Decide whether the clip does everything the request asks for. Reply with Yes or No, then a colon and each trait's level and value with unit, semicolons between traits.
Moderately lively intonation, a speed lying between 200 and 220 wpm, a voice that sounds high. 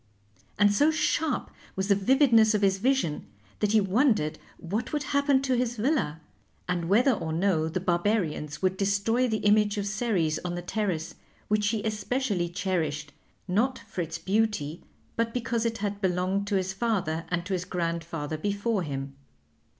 No: average, 4.6 semitones; average, 165 wpm; high, 200 Hz